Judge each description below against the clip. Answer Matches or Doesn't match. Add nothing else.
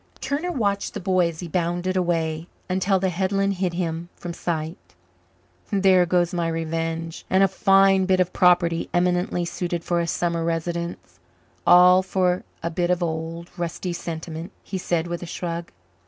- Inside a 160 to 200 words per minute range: Matches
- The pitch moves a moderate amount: Doesn't match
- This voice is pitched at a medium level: Matches